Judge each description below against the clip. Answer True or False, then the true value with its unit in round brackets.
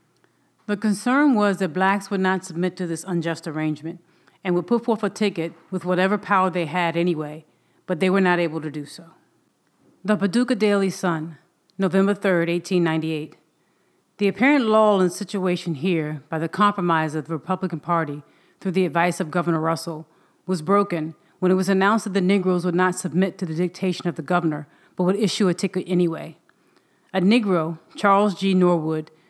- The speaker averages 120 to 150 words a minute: False (180 wpm)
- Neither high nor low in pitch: True (180 Hz)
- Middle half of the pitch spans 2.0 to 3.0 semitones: True (2.7 semitones)